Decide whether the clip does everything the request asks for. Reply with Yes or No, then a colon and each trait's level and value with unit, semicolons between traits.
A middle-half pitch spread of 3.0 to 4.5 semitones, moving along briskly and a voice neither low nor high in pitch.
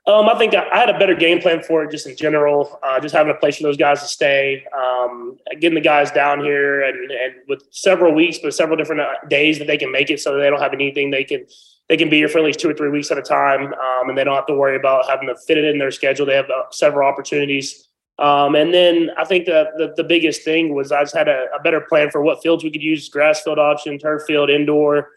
No: narrow, 2.4 semitones; fast, 275 wpm; medium, 150 Hz